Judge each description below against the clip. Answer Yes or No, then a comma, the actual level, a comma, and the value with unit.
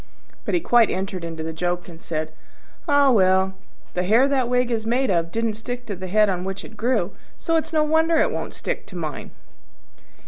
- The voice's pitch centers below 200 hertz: No, high, 215 Hz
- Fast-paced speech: Yes, fast, 210 wpm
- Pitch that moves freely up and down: Yes, wide, 5.8 semitones